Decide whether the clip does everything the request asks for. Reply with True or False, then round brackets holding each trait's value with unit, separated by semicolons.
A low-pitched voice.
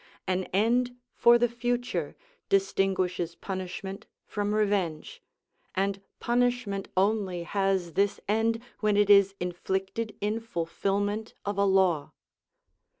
False (200 Hz)